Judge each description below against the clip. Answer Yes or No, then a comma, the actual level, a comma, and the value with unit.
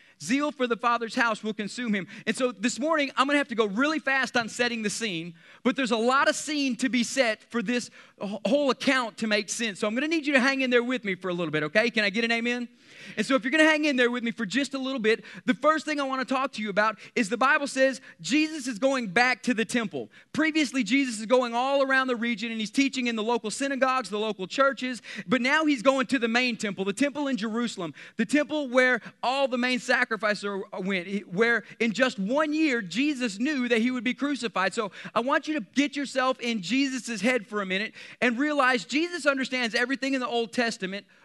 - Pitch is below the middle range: No, high, 245 Hz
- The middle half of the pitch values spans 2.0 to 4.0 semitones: Yes, average, 3.5 semitones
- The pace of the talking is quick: Yes, fast, 245 wpm